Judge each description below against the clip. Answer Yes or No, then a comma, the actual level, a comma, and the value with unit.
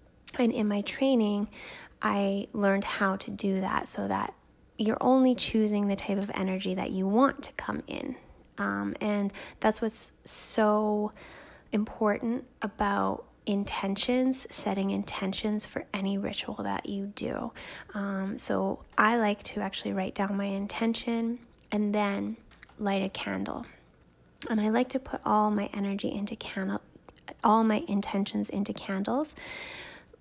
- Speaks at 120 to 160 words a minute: Yes, average, 140 wpm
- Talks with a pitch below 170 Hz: No, high, 210 Hz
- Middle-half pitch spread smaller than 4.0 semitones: Yes, narrow, 2.4 semitones